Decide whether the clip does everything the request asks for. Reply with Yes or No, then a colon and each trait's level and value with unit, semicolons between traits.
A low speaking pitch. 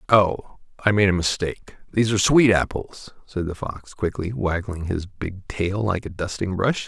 Yes: very low, 95 Hz